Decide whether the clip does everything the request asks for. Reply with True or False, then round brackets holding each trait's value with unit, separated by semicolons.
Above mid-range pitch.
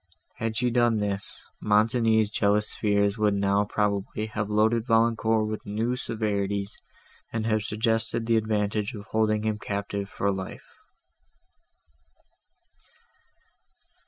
False (105 Hz)